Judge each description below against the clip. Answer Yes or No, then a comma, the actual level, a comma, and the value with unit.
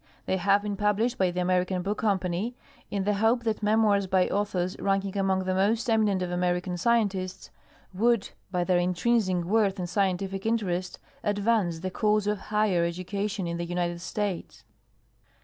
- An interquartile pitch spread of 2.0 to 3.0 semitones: Yes, narrow, 2.6 semitones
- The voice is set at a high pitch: Yes, high, 195 Hz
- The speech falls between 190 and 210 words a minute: No, average, 165 wpm